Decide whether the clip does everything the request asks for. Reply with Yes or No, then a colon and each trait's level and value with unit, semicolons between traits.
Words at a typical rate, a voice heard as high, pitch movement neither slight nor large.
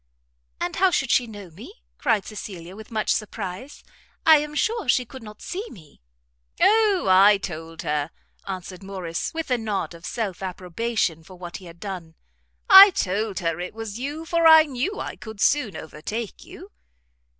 No: average, 170 wpm; high, 210 Hz; wide, 6.9 semitones